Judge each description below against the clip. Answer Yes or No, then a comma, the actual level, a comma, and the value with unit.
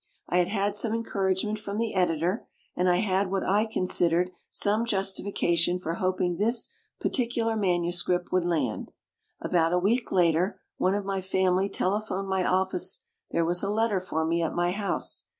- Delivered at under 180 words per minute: Yes, average, 170 wpm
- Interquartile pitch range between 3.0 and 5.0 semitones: No, narrow, 2.5 semitones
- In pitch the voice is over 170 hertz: Yes, medium, 185 Hz